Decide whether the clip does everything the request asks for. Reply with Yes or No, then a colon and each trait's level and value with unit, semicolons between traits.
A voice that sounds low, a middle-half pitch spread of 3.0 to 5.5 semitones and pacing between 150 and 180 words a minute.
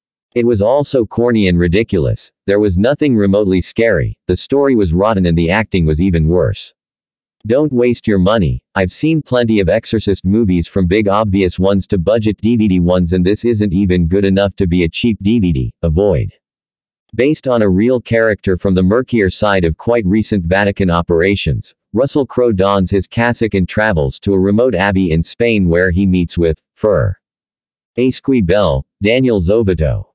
Yes: low, 100 Hz; average, 4.0 semitones; average, 170 wpm